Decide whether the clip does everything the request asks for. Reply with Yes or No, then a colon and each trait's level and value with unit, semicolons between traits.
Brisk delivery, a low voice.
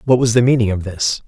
Yes: fast, 285 wpm; low, 115 Hz